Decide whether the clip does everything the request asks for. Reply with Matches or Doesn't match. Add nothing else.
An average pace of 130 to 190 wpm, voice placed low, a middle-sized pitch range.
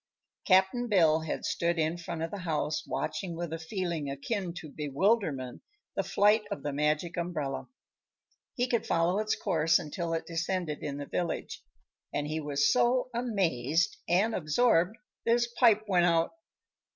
Doesn't match